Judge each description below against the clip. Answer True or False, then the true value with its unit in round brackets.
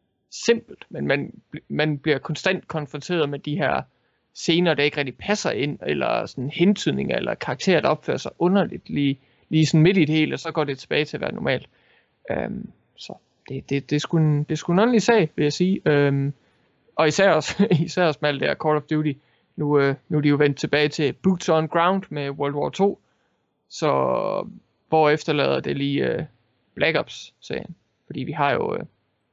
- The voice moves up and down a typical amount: True (3.5 semitones)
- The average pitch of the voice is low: False (155 Hz)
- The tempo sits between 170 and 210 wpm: True (200 wpm)